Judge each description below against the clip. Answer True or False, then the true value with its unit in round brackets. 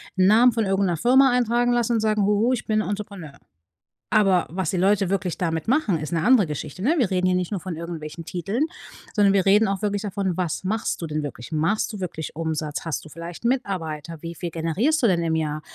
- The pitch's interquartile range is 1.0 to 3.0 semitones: False (4.5 semitones)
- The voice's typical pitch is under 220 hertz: True (190 Hz)